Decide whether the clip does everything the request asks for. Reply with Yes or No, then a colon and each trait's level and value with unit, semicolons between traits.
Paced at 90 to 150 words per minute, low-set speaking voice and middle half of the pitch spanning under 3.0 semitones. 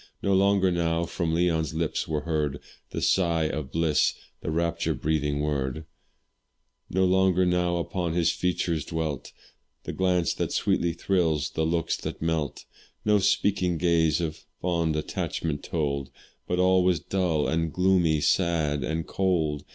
Yes: average, 145 wpm; very low, 85 Hz; narrow, 2.6 semitones